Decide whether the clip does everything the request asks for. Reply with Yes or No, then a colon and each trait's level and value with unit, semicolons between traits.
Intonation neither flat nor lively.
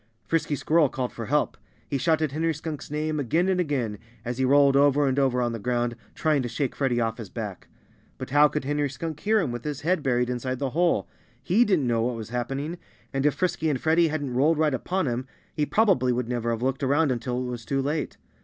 Yes: average, 3.9 semitones